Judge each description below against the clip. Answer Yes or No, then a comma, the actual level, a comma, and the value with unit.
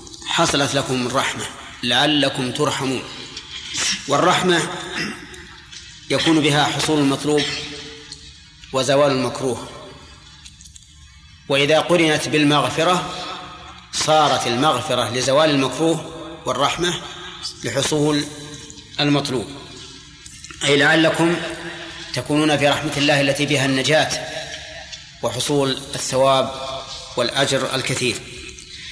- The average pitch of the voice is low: No, medium, 145 Hz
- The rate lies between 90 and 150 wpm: No, average, 75 wpm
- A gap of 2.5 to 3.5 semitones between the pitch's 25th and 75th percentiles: Yes, average, 2.8 semitones